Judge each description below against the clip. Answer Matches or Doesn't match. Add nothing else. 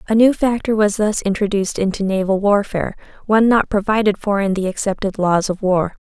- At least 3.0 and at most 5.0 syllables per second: Doesn't match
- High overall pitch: Matches